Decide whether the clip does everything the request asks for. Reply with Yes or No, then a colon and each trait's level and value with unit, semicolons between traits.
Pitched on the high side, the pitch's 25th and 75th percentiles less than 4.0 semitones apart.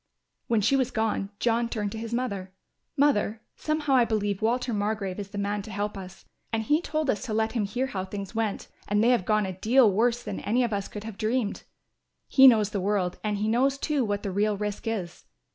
Yes: high, 215 Hz; average, 2.9 semitones